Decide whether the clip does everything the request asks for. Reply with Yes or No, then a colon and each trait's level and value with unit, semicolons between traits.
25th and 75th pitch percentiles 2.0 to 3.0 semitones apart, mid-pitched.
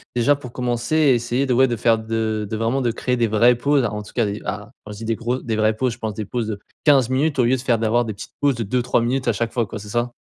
No: narrow, 2.4 semitones; low, 120 Hz